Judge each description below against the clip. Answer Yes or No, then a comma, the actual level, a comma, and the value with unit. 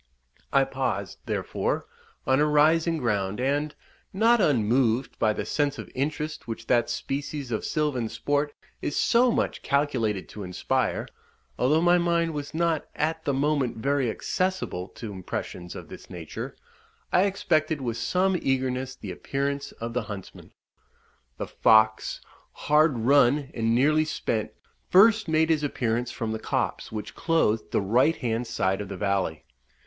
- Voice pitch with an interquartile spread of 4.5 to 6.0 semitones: Yes, wide, 5.4 semitones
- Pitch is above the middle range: No, low, 135 Hz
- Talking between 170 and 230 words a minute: No, average, 150 wpm